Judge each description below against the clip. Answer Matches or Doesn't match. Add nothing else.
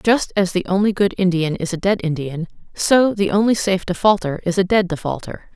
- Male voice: Doesn't match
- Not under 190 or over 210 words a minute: Matches